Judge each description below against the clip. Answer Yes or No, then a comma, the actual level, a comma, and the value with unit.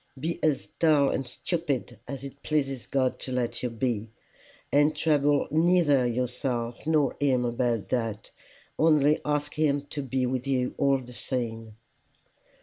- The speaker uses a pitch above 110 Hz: Yes, low, 135 Hz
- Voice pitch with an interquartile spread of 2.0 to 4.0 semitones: Yes, average, 3.1 semitones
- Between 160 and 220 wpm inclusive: No, average, 145 wpm